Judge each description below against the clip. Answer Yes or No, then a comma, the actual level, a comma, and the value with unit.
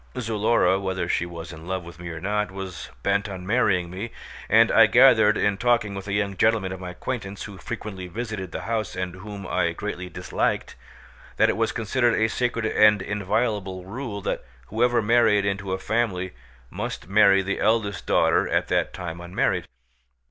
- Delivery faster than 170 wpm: Yes, average, 180 wpm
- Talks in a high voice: No, low, 100 Hz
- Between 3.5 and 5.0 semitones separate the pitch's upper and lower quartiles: No, average, 3.0 semitones